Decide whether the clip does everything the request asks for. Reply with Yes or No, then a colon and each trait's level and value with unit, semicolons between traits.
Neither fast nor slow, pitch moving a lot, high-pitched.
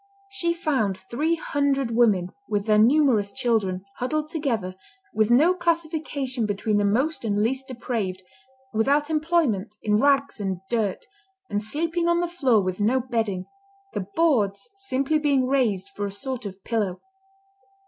Yes: average, 150 wpm; wide, 6.4 semitones; high, 240 Hz